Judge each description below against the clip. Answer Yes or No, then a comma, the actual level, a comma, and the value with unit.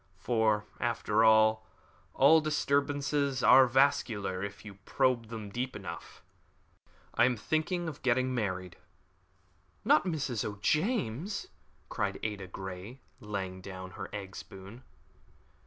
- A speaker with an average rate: No, slow, 115 wpm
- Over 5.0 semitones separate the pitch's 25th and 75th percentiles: Yes, wide, 5.5 semitones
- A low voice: Yes, low, 115 Hz